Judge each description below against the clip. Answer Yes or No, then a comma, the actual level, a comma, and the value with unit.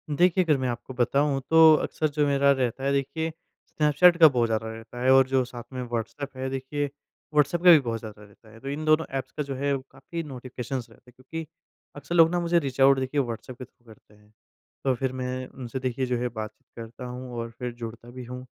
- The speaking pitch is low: Yes, low, 130 Hz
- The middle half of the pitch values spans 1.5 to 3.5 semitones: Yes, average, 3.0 semitones